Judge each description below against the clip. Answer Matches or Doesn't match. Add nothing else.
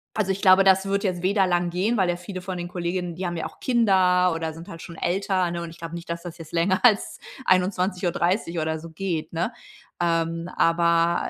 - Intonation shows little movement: Matches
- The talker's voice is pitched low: Doesn't match